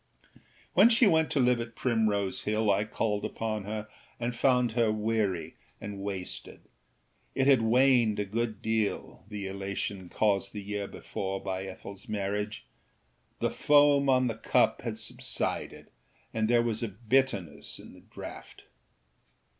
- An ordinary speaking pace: Yes, average, 145 wpm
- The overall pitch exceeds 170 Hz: No, low, 110 Hz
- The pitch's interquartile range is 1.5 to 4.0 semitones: Yes, average, 3.1 semitones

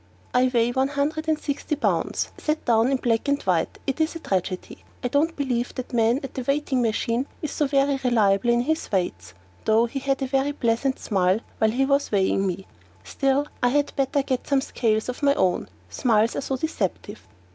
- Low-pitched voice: No, very high, 255 Hz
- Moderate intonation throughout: Yes, average, 4.1 semitones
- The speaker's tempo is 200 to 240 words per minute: Yes, fast, 205 wpm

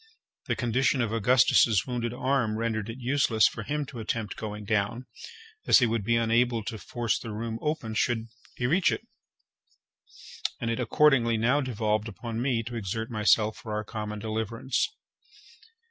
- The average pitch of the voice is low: Yes, low, 115 Hz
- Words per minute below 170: Yes, average, 160 wpm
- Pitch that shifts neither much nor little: No, narrow, 2.2 semitones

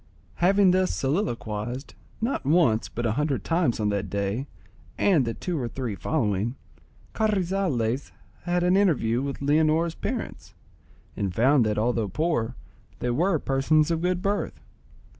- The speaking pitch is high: No, medium, 140 Hz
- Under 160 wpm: Yes, average, 140 wpm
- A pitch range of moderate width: No, wide, 7.2 semitones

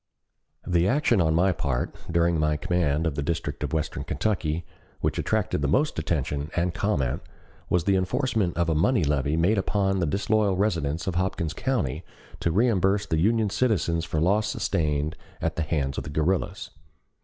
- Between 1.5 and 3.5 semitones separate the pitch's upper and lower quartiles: No, average, 4.3 semitones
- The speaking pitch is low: Yes, very low, 85 Hz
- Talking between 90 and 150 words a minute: No, average, 175 wpm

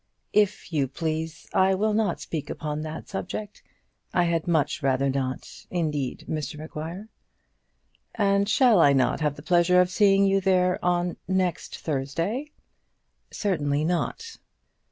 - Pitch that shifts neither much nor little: Yes, average, 4.3 semitones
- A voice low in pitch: No, medium, 175 Hz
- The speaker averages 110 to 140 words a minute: Yes, slow, 135 wpm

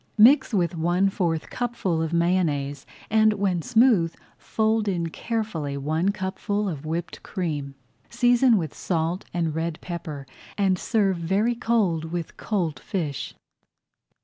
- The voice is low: No, medium, 175 Hz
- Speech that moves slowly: Yes, slow, 130 wpm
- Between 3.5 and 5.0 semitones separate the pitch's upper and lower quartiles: Yes, average, 4.5 semitones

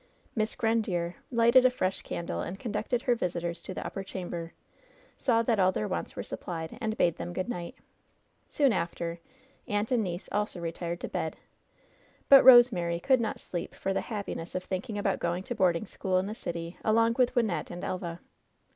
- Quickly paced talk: No, average, 185 wpm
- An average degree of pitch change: Yes, average, 4.8 semitones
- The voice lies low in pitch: No, high, 190 Hz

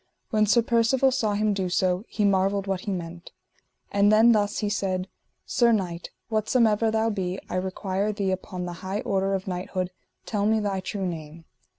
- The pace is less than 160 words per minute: No, average, 185 wpm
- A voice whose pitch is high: Yes, high, 200 Hz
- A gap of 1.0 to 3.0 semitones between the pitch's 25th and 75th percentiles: Yes, narrow, 2.6 semitones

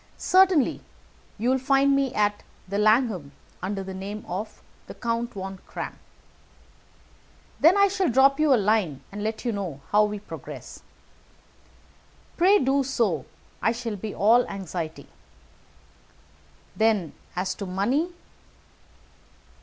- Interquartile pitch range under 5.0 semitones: No, wide, 5.4 semitones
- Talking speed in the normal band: No, slow, 130 wpm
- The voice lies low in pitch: No, high, 220 Hz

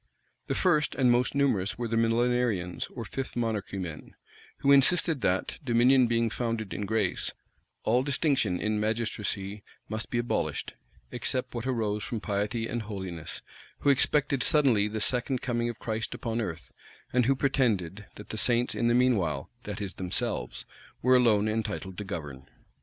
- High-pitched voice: No, low, 115 Hz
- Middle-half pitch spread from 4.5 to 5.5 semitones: No, average, 3.4 semitones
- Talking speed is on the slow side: No, average, 165 wpm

